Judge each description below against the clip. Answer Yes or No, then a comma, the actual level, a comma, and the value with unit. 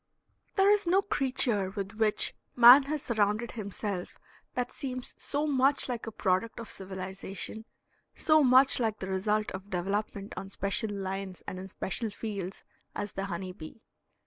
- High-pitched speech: Yes, high, 210 Hz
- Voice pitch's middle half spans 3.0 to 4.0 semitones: No, average, 4.4 semitones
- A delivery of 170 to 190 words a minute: No, average, 155 wpm